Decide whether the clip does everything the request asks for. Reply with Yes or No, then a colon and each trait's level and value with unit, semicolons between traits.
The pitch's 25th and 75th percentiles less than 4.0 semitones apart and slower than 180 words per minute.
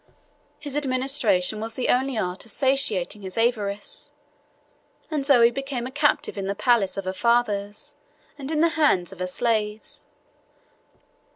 No: average, 5.2 semitones; average, 150 wpm